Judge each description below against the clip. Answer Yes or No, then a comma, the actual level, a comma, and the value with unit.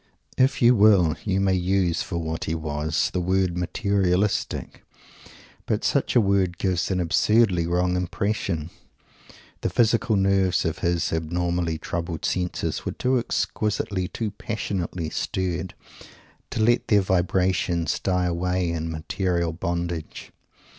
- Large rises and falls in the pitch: No, narrow, 2.4 semitones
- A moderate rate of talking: No, slow, 130 wpm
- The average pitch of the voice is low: Yes, very low, 90 Hz